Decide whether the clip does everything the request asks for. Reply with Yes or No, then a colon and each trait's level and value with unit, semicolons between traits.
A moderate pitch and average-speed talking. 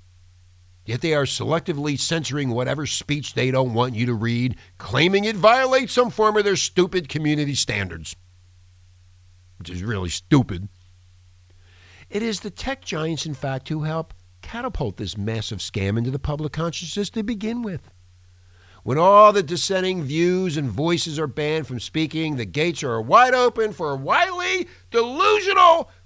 Yes: medium, 145 Hz; average, 155 wpm